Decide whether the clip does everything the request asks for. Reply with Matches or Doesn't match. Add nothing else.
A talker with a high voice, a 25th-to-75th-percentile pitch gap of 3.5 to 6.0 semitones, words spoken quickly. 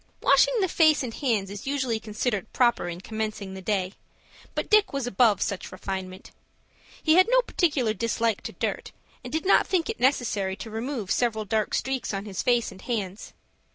Doesn't match